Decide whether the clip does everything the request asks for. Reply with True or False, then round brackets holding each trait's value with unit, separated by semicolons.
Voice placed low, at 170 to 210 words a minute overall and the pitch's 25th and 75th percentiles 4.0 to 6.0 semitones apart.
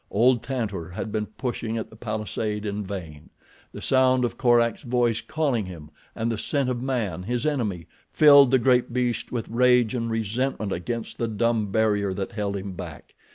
False (115 Hz; 180 wpm; 3.4 semitones)